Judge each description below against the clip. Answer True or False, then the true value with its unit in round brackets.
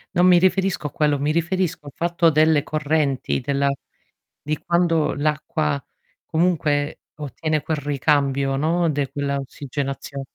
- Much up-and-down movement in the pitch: False (2.7 semitones)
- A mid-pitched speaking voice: True (150 Hz)